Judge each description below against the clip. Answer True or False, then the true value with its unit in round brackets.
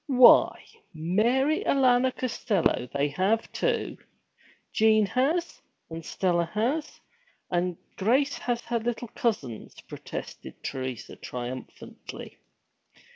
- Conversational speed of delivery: False (95 wpm)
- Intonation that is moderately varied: False (6.9 semitones)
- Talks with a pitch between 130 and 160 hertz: False (220 Hz)